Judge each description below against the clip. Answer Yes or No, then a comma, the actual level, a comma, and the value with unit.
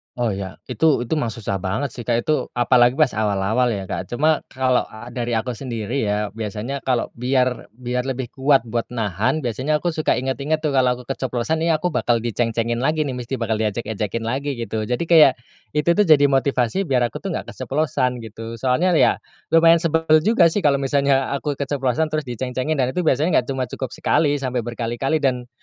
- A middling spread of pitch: Yes, average, 3.8 semitones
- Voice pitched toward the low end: Yes, low, 125 Hz